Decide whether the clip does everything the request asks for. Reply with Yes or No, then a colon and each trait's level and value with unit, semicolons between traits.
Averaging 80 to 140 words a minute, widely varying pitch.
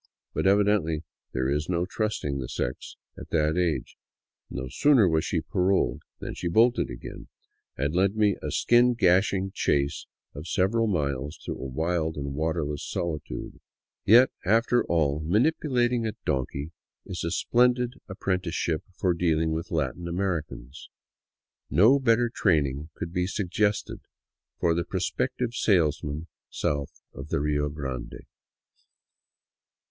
Yes: slow, 135 wpm; wide, 5.7 semitones